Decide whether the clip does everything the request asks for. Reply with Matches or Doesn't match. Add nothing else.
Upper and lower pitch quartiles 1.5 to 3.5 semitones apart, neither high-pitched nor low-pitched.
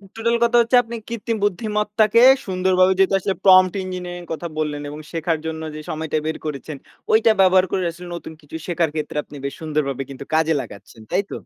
Doesn't match